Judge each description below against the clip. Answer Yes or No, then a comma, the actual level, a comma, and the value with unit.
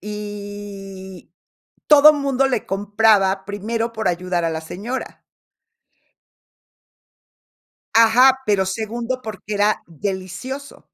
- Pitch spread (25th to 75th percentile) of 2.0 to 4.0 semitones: Yes, average, 3.4 semitones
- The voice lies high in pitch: Yes, high, 205 Hz